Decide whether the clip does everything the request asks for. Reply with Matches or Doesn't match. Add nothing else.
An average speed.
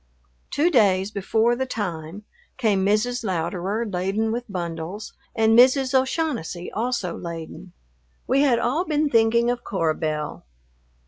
Doesn't match